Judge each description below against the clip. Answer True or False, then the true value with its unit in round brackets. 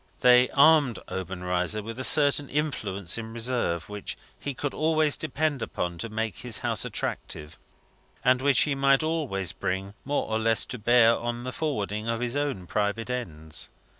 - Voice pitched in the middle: False (120 Hz)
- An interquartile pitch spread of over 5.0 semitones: True (5.5 semitones)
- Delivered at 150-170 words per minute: True (165 wpm)